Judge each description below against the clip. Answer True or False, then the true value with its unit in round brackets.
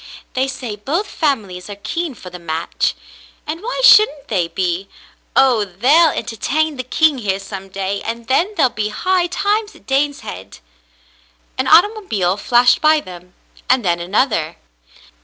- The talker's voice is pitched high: True (240 Hz)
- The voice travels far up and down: True (8.5 semitones)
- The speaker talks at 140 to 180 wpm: True (160 wpm)